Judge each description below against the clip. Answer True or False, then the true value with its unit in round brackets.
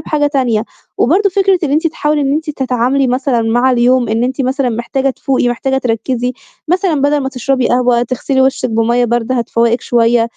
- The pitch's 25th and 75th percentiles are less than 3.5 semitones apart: True (2.7 semitones)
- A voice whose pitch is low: False (255 Hz)